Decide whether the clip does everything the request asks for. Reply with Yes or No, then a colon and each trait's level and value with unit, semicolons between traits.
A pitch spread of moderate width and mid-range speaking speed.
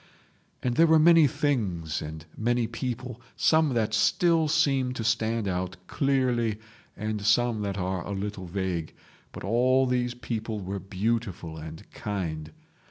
Yes: average, 4.9 semitones; average, 145 wpm